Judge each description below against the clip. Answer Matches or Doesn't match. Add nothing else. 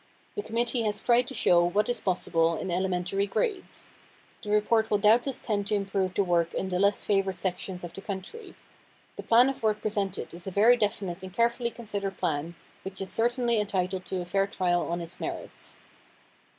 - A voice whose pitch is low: Doesn't match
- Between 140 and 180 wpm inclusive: Doesn't match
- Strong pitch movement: Doesn't match